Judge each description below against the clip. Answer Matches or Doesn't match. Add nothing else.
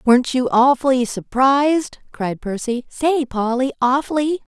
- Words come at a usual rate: Doesn't match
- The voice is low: Doesn't match